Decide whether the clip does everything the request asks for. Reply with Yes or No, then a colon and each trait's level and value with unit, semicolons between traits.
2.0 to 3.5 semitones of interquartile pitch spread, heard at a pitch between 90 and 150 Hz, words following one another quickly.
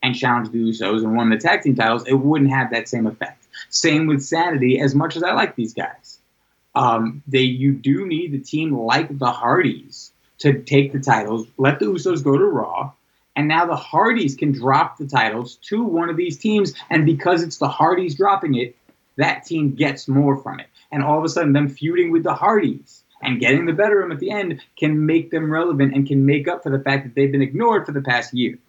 No: average, 4.0 semitones; medium, 140 Hz; fast, 230 wpm